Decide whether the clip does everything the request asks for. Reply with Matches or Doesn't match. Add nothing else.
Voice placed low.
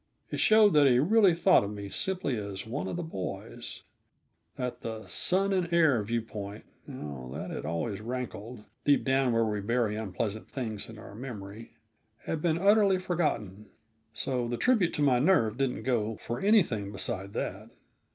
Matches